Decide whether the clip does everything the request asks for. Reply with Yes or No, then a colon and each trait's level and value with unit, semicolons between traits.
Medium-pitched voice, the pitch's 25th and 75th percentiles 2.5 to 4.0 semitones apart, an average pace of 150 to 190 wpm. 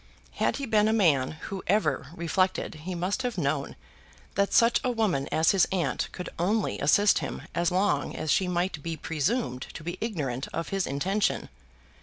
No: medium, 180 Hz; average, 4.7 semitones; average, 180 wpm